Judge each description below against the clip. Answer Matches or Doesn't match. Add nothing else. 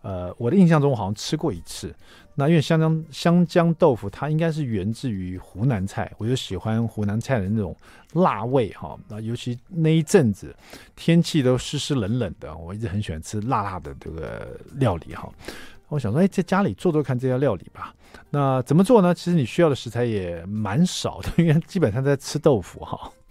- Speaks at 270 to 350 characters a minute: Matches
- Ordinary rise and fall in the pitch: Doesn't match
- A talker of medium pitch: Doesn't match